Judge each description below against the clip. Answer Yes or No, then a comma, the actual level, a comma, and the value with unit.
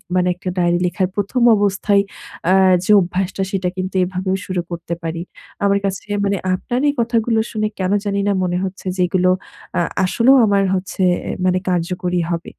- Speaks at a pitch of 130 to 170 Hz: No, medium, 185 Hz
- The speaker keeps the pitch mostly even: Yes, narrow, 1.9 semitones